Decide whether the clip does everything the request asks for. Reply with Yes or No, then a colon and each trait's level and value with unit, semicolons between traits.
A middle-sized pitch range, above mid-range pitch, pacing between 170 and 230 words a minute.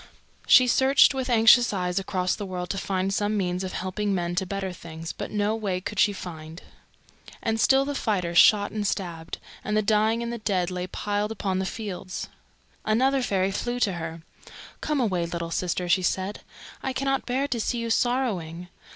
Yes: average, 3.9 semitones; high, 200 Hz; average, 190 wpm